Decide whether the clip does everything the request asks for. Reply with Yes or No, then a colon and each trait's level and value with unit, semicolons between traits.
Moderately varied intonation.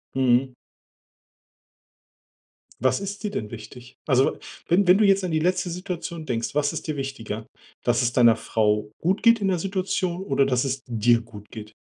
No: wide, 7.6 semitones